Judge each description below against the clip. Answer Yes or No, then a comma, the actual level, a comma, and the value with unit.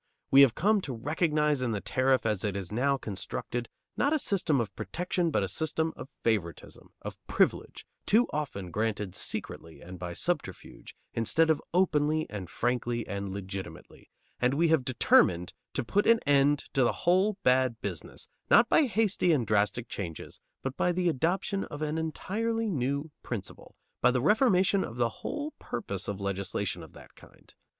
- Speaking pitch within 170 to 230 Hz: No, low, 130 Hz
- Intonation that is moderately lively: No, wide, 8.2 semitones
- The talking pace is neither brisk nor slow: Yes, average, 170 wpm